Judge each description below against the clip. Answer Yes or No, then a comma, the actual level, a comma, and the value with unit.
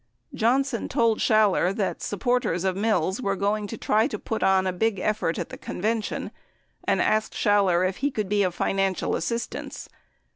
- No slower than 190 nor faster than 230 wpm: No, average, 175 wpm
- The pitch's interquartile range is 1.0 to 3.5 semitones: Yes, average, 2.9 semitones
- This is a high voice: Yes, high, 205 Hz